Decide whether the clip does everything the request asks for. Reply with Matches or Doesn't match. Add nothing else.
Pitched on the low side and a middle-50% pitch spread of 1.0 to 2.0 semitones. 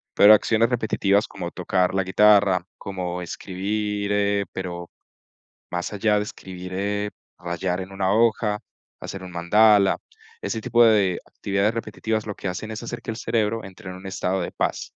Doesn't match